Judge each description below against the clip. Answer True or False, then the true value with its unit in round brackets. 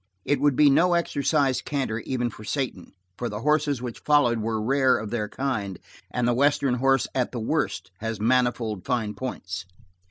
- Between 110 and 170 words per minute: False (180 wpm)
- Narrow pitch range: False (3.9 semitones)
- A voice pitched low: True (125 Hz)